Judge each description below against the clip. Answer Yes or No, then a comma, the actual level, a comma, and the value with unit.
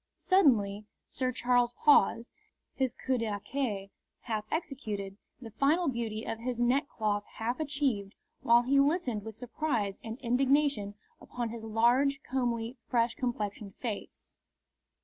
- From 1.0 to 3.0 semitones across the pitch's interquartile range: No, average, 3.7 semitones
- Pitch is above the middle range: Yes, high, 240 Hz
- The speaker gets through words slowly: Yes, slow, 130 wpm